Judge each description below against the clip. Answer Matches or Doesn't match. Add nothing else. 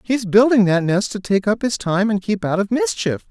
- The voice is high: Matches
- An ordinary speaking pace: Doesn't match